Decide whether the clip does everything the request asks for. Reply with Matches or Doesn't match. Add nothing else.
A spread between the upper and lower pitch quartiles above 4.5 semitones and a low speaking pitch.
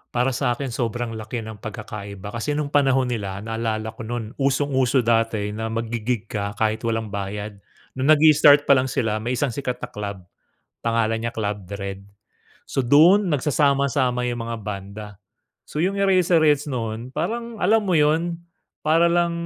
Matches